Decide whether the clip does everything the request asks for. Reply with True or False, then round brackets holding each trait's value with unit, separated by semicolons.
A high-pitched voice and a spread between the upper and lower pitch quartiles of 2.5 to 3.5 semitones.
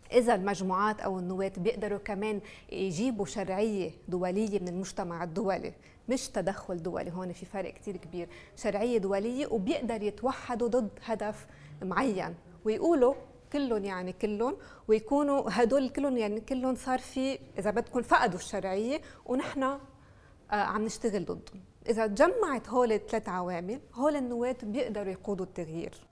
False (215 Hz; 4.4 semitones)